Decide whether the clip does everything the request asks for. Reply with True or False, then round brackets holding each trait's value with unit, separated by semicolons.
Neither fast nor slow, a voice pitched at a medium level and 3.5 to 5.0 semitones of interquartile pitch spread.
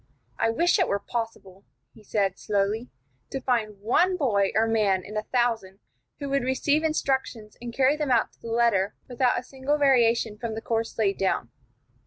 False (185 wpm; 230 Hz; 3.9 semitones)